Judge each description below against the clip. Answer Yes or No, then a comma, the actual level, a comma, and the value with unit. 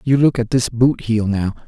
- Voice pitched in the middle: No, low, 115 Hz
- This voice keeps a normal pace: No, fast, 250 wpm